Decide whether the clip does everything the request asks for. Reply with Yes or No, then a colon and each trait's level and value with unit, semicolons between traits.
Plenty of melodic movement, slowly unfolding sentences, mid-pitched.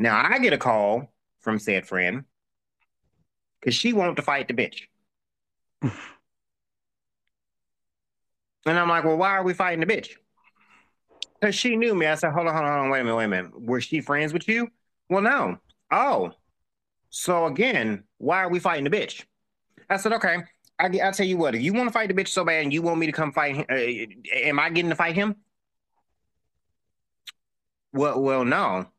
No: wide, 5.9 semitones; average, 195 wpm; medium, 165 Hz